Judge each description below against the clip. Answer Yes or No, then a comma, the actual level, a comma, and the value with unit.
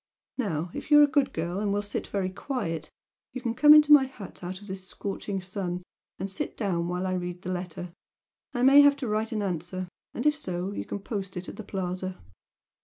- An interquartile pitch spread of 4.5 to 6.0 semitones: Yes, average, 4.9 semitones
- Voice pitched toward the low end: No, high, 195 Hz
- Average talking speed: No, fast, 225 wpm